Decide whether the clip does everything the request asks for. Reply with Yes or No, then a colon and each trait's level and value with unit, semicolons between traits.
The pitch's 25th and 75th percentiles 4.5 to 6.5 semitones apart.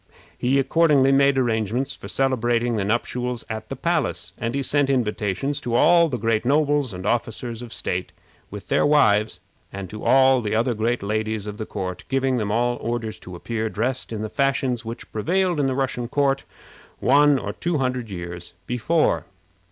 No: average, 3.9 semitones